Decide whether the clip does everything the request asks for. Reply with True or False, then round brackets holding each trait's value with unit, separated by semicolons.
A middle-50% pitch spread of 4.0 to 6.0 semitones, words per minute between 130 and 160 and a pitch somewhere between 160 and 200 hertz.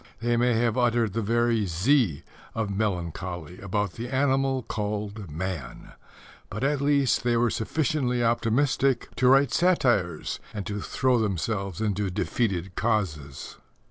False (4.3 semitones; 135 wpm; 110 Hz)